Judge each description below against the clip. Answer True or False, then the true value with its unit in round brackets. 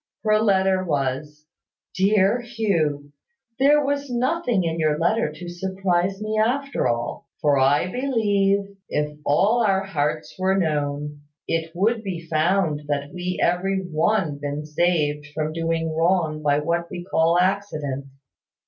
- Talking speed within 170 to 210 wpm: False (140 wpm)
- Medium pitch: True (175 Hz)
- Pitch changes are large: False (4.7 semitones)